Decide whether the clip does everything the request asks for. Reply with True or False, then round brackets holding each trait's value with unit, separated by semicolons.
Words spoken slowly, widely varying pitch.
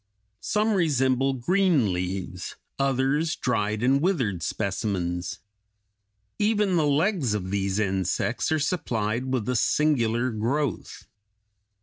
True (105 wpm; 6.6 semitones)